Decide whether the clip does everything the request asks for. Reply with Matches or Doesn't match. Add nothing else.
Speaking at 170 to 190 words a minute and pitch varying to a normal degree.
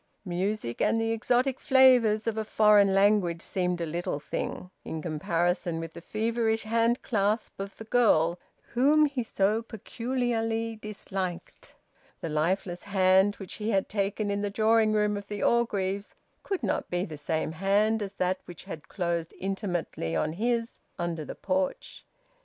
Doesn't match